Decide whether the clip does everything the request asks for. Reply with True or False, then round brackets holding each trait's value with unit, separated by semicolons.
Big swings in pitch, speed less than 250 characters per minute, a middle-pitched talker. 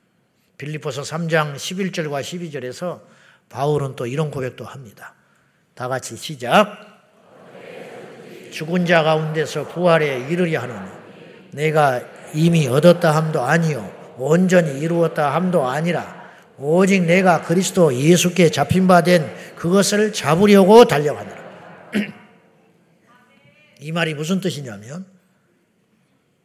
False (3.4 semitones; 235 characters per minute; 165 Hz)